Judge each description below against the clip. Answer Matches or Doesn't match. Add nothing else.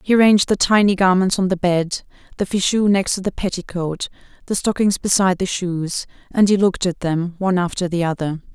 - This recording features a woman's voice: Matches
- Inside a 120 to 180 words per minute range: Doesn't match